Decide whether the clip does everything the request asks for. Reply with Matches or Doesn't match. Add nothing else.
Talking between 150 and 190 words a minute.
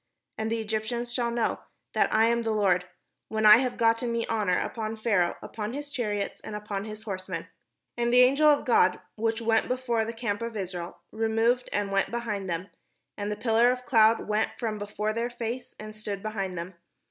Doesn't match